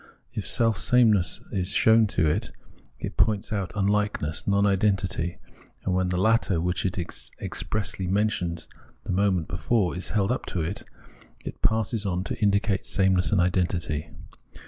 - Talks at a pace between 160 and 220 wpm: No, average, 150 wpm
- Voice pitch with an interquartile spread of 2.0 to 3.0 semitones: Yes, average, 2.7 semitones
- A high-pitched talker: No, very low, 95 Hz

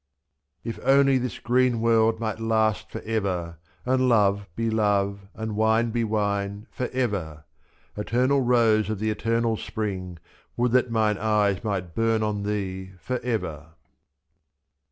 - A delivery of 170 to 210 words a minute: No, average, 145 wpm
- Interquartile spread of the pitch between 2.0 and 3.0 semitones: Yes, narrow, 2.5 semitones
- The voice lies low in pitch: Yes, low, 110 Hz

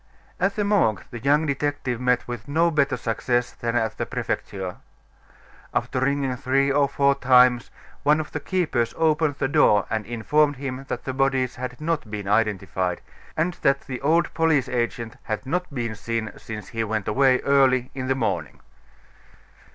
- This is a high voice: No, low, 130 Hz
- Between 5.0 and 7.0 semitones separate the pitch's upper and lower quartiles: No, average, 3.9 semitones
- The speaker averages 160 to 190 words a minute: Yes, average, 170 wpm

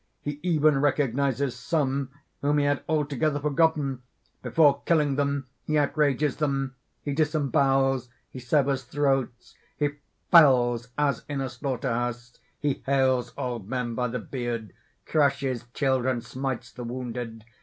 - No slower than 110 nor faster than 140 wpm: Yes, slow, 135 wpm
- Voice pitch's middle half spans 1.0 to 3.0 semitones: Yes, average, 2.7 semitones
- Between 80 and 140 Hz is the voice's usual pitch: Yes, low, 135 Hz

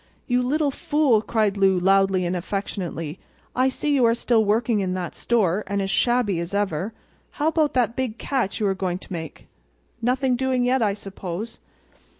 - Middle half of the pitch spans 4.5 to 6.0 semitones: Yes, average, 4.8 semitones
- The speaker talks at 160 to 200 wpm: Yes, average, 180 wpm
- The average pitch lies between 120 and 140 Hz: No, high, 210 Hz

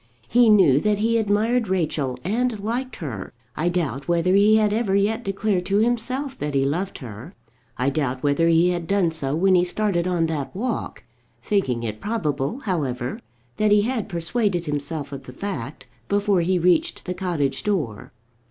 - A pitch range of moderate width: No, wide, 6.2 semitones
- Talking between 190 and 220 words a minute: No, average, 175 wpm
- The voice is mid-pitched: Yes, medium, 180 Hz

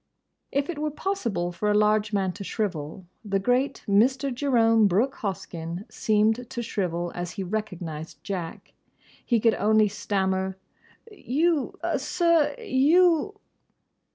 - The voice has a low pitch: No, high, 215 Hz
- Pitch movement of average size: No, wide, 6.0 semitones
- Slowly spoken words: Yes, slow, 125 wpm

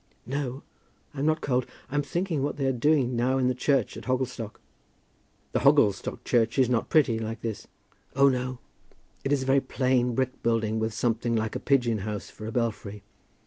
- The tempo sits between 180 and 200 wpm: Yes, average, 185 wpm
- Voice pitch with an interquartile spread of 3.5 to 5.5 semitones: No, average, 3.1 semitones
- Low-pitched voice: Yes, low, 125 Hz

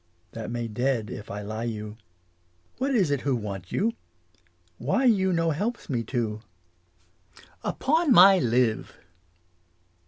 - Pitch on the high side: No, low, 125 Hz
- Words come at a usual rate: No, slow, 130 wpm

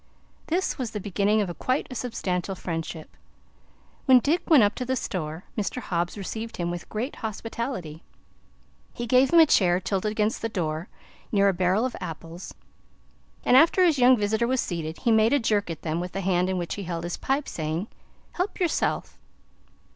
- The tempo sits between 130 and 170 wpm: No, average, 185 wpm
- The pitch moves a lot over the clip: Yes, wide, 6.1 semitones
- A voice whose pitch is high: Yes, high, 205 Hz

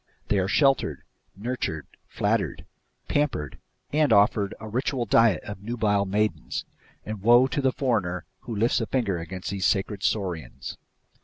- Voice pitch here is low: Yes, low, 105 Hz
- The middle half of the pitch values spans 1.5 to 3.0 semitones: No, average, 3.9 semitones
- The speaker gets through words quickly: No, average, 145 wpm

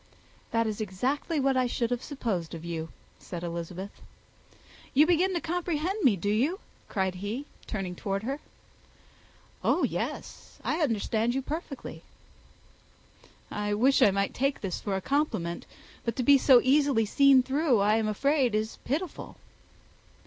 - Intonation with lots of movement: Yes, wide, 6.0 semitones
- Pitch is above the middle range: Yes, high, 240 Hz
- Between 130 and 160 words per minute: Yes, average, 150 wpm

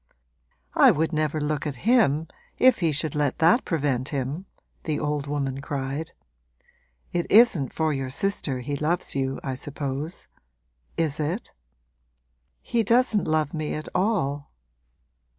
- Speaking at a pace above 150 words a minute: No, slow, 135 wpm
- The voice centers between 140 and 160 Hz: Yes, medium, 150 Hz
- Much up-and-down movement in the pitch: No, average, 3.3 semitones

